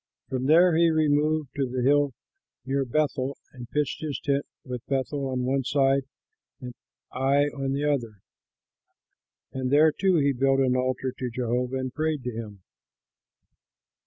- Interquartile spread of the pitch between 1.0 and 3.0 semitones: Yes, narrow, 2.4 semitones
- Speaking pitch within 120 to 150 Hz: Yes, low, 135 Hz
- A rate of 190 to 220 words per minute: No, average, 155 wpm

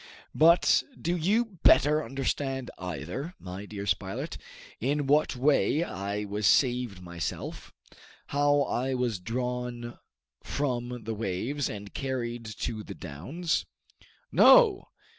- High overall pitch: No, low, 125 Hz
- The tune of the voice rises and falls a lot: Yes, wide, 6.0 semitones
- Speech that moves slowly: Yes, slow, 115 wpm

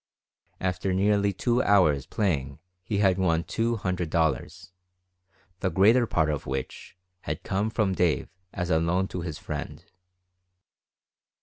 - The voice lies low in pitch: Yes, very low, 95 Hz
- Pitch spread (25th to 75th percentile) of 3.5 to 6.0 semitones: Yes, average, 3.8 semitones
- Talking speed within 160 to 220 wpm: No, slow, 135 wpm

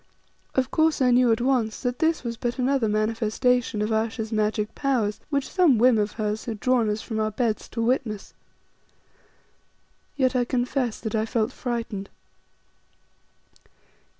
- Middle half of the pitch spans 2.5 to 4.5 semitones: Yes, average, 2.8 semitones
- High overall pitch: Yes, high, 235 Hz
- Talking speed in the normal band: Yes, average, 150 wpm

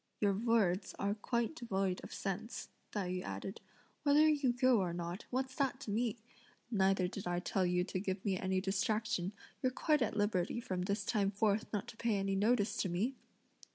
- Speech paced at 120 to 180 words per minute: No, average, 190 wpm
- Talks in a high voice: Yes, high, 205 Hz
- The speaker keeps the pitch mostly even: No, average, 3.8 semitones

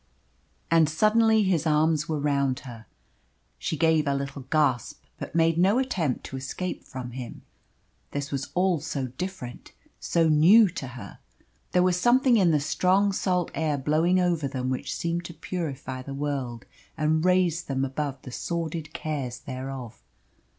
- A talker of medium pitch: Yes, medium, 155 Hz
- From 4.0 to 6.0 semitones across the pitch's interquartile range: Yes, average, 4.7 semitones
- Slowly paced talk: No, average, 155 wpm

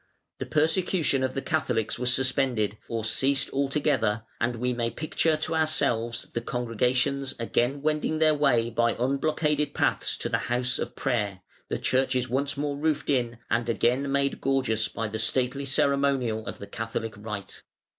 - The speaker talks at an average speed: Yes, average, 160 wpm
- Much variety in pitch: No, average, 3.4 semitones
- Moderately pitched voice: No, low, 130 Hz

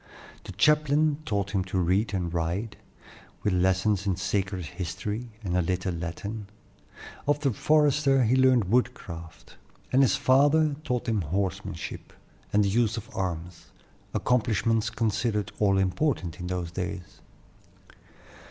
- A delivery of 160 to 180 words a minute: No, slow, 135 wpm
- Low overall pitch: Yes, low, 100 Hz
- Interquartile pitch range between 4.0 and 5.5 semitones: Yes, average, 5.2 semitones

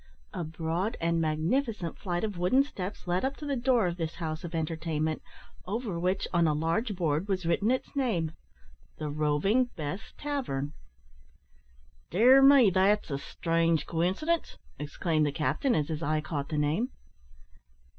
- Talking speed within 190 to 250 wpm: No, average, 155 wpm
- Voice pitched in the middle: Yes, medium, 170 Hz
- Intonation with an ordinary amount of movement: No, wide, 5.7 semitones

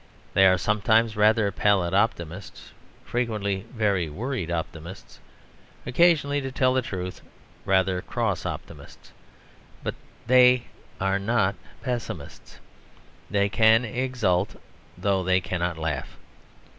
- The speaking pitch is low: Yes, low, 100 Hz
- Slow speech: Yes, slow, 105 wpm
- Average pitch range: Yes, average, 4.5 semitones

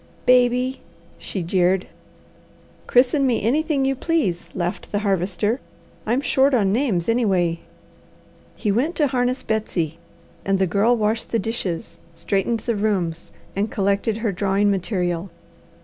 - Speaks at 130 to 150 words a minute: Yes, slow, 135 wpm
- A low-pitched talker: No, high, 210 Hz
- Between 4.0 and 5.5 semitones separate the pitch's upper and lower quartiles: Yes, average, 4.6 semitones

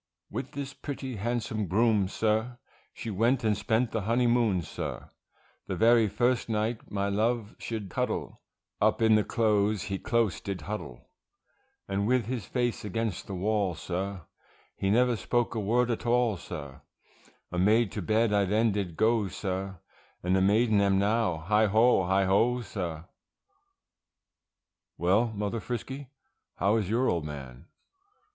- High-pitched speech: No, low, 105 Hz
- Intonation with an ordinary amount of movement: Yes, average, 3.2 semitones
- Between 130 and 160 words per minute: Yes, average, 150 wpm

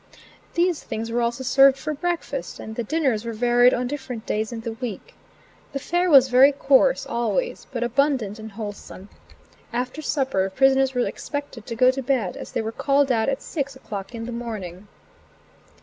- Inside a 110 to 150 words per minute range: No, average, 180 wpm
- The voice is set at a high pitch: Yes, very high, 250 Hz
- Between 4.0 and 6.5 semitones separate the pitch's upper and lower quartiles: No, average, 3.5 semitones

